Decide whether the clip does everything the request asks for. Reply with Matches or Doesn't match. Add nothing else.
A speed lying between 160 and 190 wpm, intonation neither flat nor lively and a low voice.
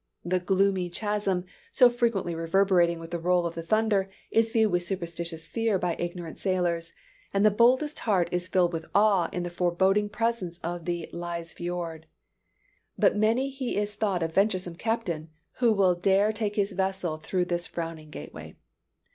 Doesn't match